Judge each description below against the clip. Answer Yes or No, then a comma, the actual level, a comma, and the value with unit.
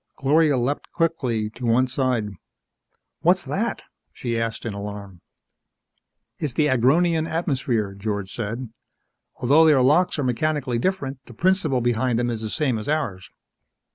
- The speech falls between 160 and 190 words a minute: No, average, 140 wpm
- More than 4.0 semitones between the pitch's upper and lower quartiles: Yes, average, 4.9 semitones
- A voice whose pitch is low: Yes, low, 125 Hz